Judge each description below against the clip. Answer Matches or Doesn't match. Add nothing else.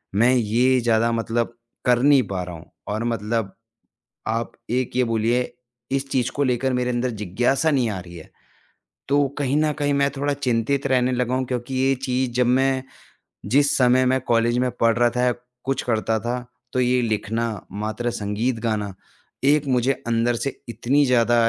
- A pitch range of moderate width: Doesn't match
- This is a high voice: Doesn't match